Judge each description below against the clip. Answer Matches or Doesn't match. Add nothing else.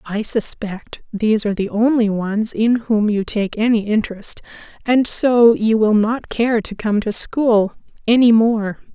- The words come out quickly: Doesn't match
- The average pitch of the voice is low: Doesn't match